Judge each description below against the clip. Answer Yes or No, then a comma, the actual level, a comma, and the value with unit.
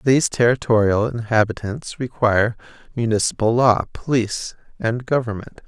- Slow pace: Yes, slow, 95 wpm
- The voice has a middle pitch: No, low, 115 Hz